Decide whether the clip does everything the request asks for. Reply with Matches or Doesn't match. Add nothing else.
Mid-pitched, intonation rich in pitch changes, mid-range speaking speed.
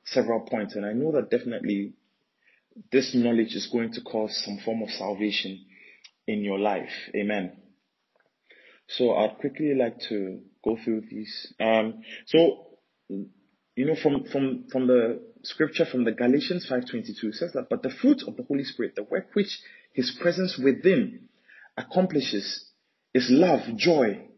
Doesn't match